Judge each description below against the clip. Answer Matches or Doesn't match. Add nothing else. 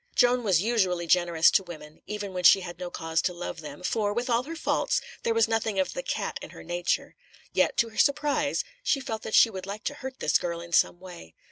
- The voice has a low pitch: Doesn't match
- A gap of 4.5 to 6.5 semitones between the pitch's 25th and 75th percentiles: Matches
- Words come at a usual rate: Doesn't match